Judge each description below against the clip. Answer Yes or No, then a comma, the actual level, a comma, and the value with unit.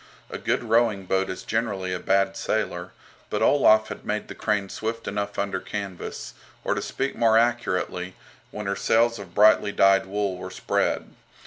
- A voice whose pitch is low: Yes, low, 100 Hz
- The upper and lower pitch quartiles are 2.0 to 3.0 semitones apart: Yes, narrow, 2.6 semitones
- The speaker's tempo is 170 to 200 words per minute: Yes, average, 175 wpm